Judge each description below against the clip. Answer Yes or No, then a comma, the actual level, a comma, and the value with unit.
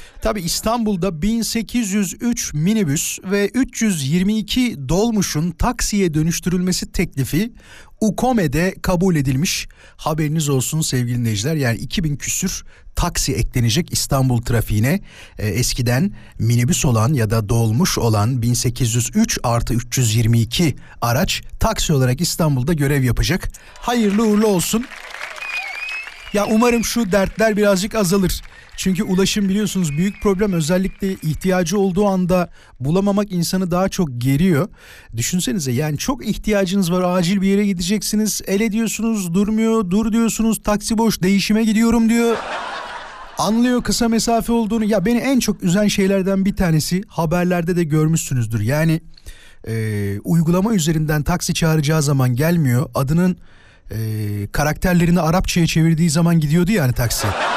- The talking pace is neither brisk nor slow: Yes, average, 120 wpm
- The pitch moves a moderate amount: No, wide, 7.2 semitones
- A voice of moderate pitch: Yes, medium, 180 Hz